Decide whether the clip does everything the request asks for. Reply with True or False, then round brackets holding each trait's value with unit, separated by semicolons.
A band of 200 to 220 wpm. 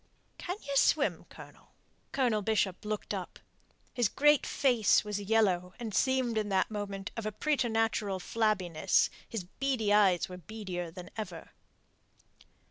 False (135 wpm)